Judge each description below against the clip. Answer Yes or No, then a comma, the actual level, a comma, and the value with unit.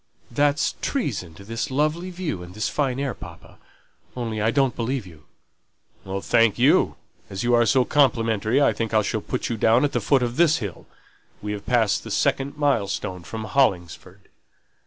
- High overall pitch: No, low, 120 Hz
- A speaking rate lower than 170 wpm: No, average, 180 wpm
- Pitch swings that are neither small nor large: Yes, average, 4.7 semitones